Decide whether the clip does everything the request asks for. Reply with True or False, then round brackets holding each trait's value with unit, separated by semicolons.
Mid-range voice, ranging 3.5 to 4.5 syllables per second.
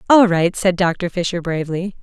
False (180 Hz; 5.1 syllables/s)